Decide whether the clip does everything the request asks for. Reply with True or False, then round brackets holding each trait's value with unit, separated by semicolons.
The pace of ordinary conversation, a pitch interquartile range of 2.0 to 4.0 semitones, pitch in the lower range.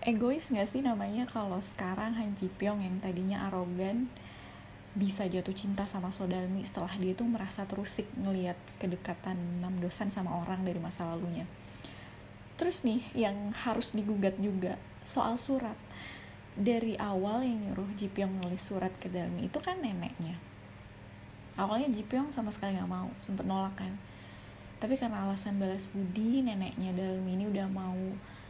False (150 wpm; 3.3 semitones; 195 Hz)